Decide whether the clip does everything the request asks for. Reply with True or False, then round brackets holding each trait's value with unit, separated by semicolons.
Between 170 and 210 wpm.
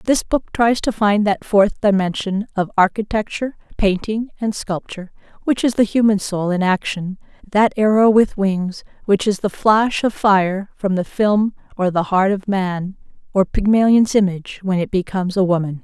True (175 wpm)